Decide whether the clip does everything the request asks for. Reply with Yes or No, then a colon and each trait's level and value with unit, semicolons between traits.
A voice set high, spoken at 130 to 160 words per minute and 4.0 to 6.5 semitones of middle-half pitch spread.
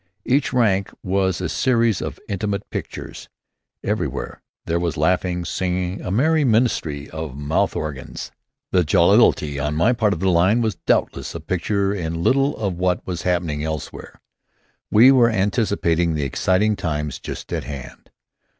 No: very low, 90 Hz; average, 155 wpm; average, 4.8 semitones